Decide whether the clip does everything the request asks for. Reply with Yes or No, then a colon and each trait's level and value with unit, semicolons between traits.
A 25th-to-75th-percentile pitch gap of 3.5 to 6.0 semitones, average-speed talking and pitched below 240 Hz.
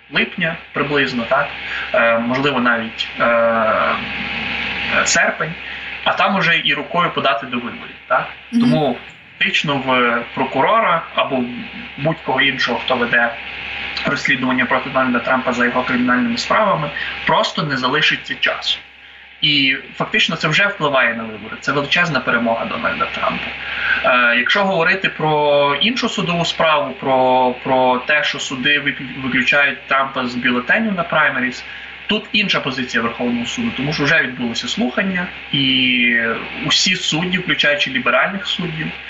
Yes: average, 4.0 semitones; average, 130 wpm; low, 135 Hz